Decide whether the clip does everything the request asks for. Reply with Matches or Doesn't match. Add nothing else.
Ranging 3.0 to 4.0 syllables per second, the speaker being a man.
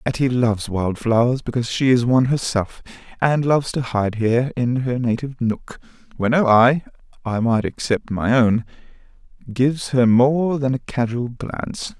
Doesn't match